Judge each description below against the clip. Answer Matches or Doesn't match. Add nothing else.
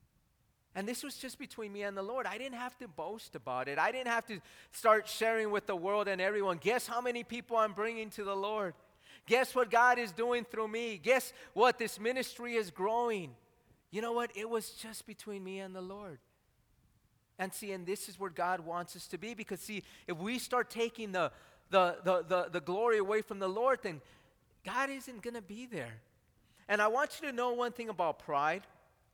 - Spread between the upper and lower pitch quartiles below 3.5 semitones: Doesn't match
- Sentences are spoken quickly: Matches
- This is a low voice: Doesn't match